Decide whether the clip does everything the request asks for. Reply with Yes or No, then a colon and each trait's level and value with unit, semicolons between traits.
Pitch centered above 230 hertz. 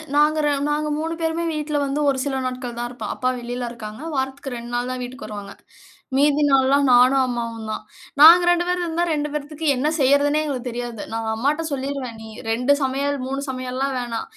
Yes: very high, 265 Hz